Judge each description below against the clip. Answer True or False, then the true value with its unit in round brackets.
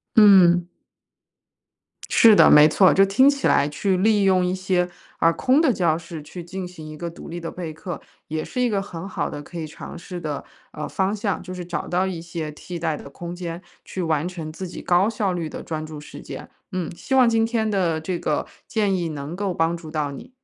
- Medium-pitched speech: True (175 Hz)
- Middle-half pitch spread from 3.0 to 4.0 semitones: True (3.3 semitones)